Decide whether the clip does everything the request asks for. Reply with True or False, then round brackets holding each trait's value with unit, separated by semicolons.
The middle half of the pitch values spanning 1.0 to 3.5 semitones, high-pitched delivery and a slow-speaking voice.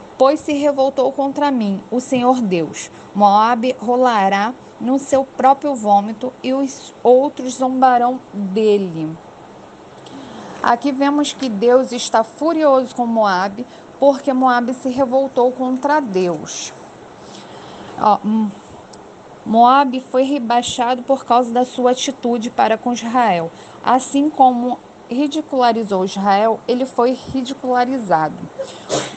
True (3.0 semitones; 250 Hz; 105 wpm)